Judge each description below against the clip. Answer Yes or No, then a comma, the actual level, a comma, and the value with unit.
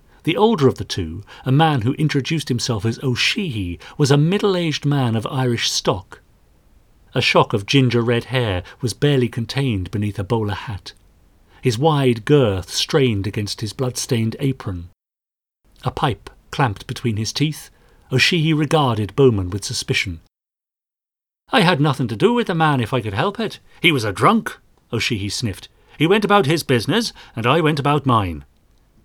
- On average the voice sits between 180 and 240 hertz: No, low, 125 Hz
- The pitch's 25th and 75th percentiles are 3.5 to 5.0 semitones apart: No, wide, 5.5 semitones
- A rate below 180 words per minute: Yes, average, 165 wpm